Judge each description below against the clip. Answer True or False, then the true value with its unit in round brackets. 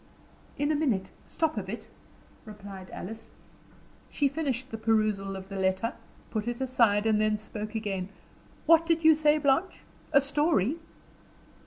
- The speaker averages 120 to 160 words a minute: True (150 wpm)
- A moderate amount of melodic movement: False (5.9 semitones)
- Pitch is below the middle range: False (225 Hz)